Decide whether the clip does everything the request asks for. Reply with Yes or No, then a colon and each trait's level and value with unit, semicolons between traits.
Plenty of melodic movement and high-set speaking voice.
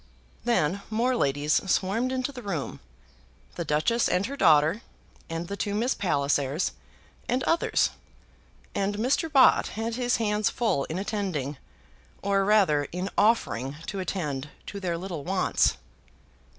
Yes: wide, 6.7 semitones; high, 195 Hz